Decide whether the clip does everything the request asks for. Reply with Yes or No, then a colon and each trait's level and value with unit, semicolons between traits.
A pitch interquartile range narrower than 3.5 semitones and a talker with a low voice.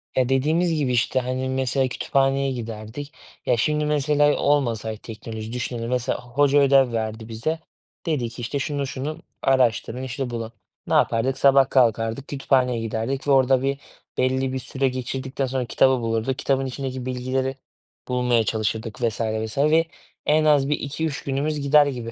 Yes: average, 2.8 semitones; low, 130 Hz